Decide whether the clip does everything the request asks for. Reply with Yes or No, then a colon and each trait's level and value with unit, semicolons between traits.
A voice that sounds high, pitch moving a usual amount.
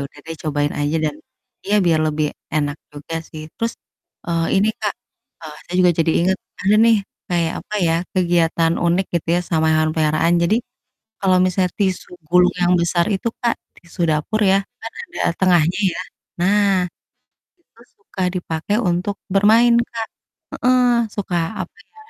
No: medium, 175 Hz; average, 3.7 semitones